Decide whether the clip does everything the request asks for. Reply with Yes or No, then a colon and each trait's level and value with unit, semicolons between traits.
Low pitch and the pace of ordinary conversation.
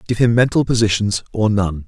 Yes: low, 105 Hz; average, 190 wpm